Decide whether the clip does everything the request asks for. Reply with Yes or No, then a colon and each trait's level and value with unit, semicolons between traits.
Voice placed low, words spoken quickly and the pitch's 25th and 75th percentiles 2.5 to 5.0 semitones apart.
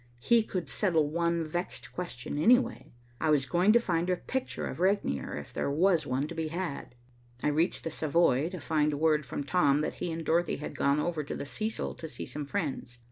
No: medium, 160 Hz; fast, 210 wpm; average, 3.4 semitones